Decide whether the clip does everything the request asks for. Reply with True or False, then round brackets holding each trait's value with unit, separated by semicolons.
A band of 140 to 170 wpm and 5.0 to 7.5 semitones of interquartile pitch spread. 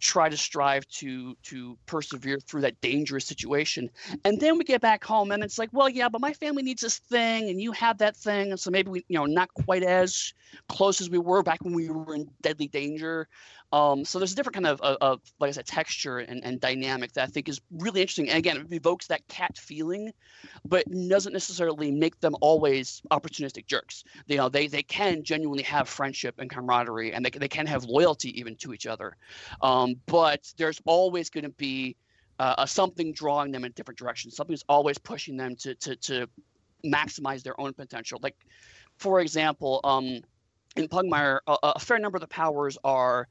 False (205 wpm; 5.4 semitones)